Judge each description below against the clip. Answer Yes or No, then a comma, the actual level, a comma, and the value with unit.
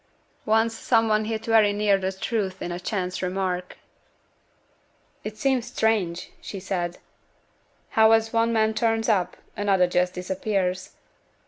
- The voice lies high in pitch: Yes, high, 205 Hz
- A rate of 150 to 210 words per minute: No, slow, 135 wpm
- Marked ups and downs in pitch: No, average, 3.3 semitones